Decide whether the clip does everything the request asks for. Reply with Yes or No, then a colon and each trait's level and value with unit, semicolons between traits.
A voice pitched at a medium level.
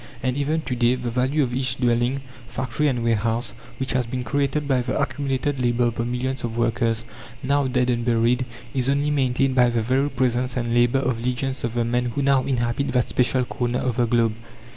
No: low, 125 Hz